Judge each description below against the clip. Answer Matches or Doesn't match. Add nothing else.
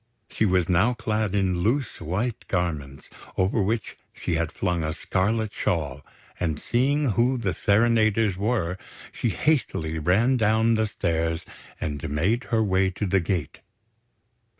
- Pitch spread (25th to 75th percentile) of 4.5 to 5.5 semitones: Matches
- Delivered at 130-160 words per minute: Matches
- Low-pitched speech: Matches